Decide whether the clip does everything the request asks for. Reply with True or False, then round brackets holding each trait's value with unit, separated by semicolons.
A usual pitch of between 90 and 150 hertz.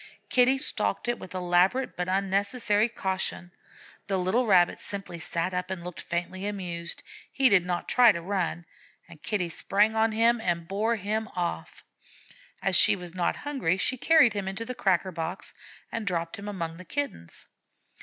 False (190 Hz)